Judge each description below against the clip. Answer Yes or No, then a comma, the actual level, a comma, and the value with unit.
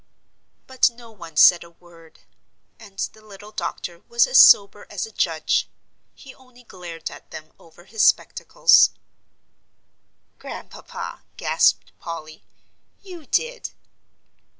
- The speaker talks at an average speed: No, slow, 120 wpm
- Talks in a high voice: Yes, high, 200 Hz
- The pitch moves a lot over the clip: Yes, wide, 6.6 semitones